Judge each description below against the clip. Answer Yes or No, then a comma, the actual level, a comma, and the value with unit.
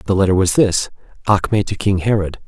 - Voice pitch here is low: Yes, very low, 95 Hz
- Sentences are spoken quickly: No, average, 195 wpm